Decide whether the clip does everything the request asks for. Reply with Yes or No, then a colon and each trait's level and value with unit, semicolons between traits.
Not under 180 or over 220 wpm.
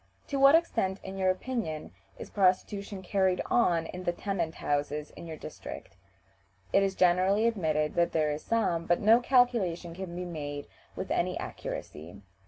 No: average, 165 wpm